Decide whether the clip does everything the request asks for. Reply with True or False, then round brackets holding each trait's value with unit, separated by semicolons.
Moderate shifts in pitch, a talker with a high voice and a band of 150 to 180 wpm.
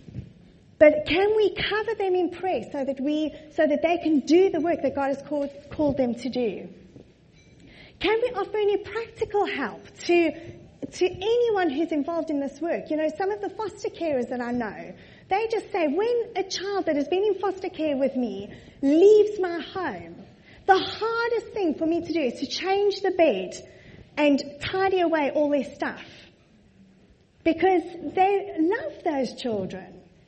True (5.0 semitones; 335 Hz; 175 wpm)